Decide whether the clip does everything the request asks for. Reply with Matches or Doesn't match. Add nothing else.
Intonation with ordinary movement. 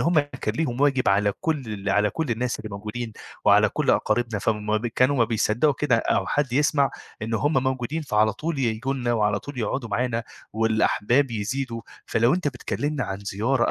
Matches